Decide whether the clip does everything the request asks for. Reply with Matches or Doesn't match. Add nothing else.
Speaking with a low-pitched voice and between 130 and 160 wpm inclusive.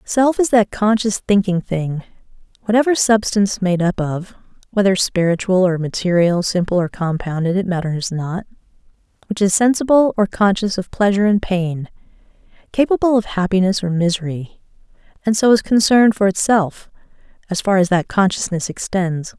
Doesn't match